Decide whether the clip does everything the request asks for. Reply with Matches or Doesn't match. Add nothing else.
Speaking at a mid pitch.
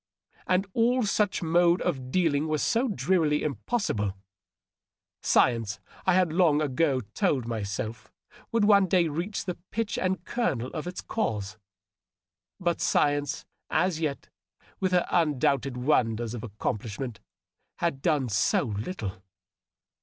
Matches